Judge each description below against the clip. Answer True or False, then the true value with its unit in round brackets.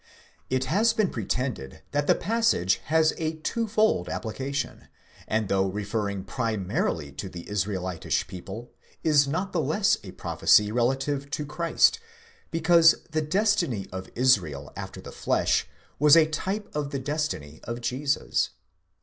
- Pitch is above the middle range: False (135 Hz)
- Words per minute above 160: False (140 wpm)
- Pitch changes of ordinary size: False (7.9 semitones)